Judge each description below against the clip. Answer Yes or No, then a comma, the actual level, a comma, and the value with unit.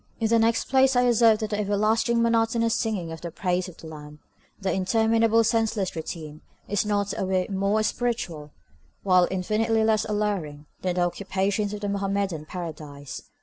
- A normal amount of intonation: Yes, average, 3.8 semitones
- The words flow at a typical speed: Yes, average, 170 wpm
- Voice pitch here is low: No, high, 200 Hz